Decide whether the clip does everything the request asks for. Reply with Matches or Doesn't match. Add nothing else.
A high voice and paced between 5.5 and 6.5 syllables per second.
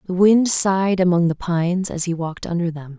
Doesn't match